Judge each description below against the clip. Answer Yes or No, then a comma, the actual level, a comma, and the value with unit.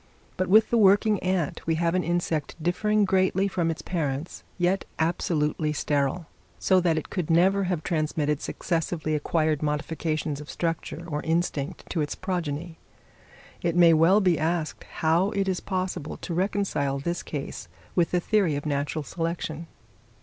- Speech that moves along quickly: No, average, 155 wpm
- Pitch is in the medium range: Yes, medium, 170 Hz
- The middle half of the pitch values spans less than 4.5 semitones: Yes, average, 3.0 semitones